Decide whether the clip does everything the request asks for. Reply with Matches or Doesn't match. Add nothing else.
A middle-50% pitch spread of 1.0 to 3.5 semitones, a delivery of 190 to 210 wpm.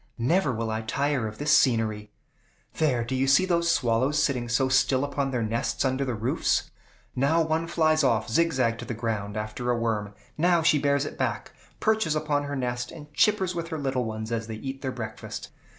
Doesn't match